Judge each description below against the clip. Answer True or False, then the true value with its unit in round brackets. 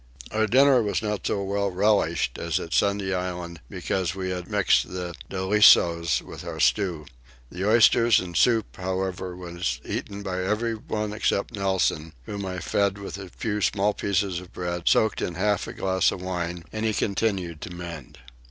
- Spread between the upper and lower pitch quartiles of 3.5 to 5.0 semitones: False (2.7 semitones)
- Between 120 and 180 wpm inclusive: True (170 wpm)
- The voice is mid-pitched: False (95 Hz)